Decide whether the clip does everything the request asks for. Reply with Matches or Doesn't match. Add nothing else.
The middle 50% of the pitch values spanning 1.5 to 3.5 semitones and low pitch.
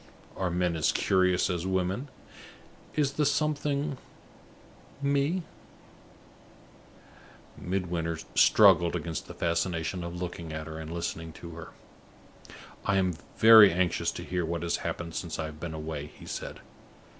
Matches